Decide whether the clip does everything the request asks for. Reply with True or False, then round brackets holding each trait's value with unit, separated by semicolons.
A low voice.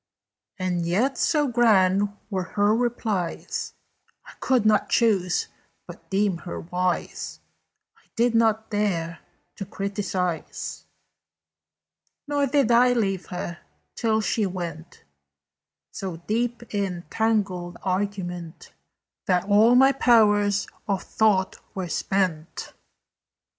False (200 Hz)